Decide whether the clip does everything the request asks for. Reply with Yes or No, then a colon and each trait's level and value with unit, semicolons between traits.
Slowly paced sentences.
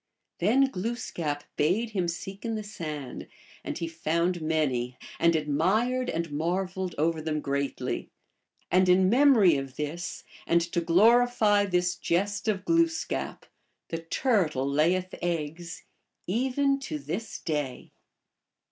Yes: slow, 130 wpm